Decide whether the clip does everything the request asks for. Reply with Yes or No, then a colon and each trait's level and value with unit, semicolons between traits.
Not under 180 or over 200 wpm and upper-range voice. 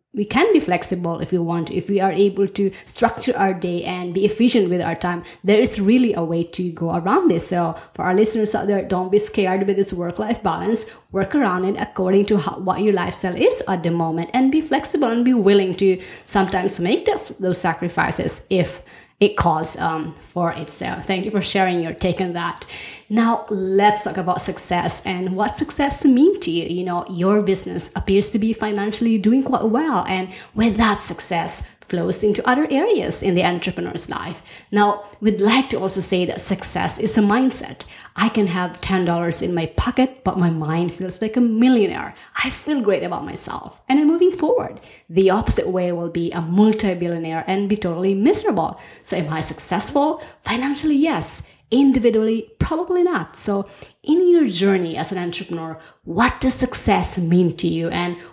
Yes: average, 190 wpm; high, 195 Hz